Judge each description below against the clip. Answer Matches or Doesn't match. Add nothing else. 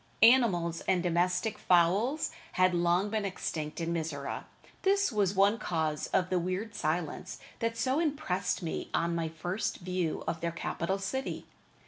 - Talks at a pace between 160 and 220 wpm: Doesn't match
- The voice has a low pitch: Doesn't match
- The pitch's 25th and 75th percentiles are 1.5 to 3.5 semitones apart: Doesn't match